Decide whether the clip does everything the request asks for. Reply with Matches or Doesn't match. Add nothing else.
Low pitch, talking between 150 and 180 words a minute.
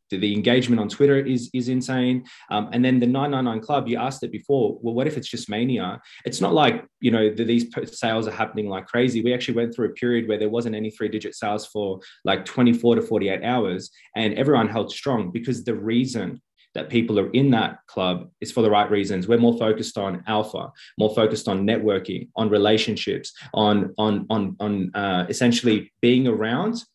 Doesn't match